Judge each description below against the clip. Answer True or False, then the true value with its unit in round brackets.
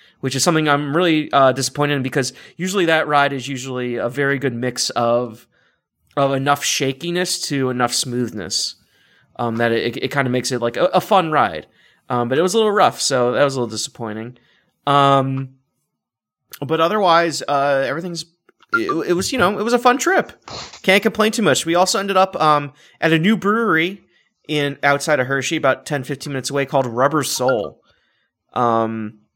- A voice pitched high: False (140 Hz)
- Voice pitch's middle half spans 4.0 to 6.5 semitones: True (5.1 semitones)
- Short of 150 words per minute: False (190 wpm)